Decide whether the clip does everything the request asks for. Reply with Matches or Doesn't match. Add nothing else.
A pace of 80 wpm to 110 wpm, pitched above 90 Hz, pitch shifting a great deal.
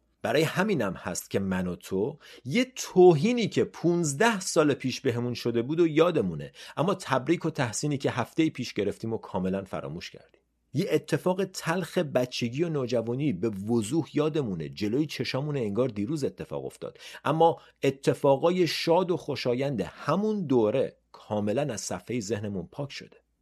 Doesn't match